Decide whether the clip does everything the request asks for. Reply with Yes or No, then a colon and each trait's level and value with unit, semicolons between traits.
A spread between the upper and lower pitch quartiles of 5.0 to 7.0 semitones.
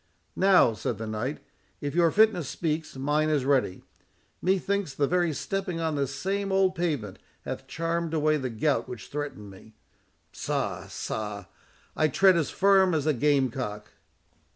Yes: wide, 5.4 semitones